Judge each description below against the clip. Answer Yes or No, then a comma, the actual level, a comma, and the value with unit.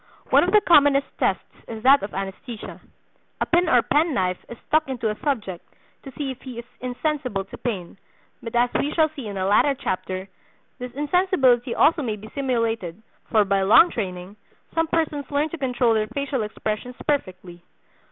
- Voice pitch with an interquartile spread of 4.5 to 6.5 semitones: Yes, wide, 5.4 semitones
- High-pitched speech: Yes, high, 245 Hz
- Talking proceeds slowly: No, average, 180 wpm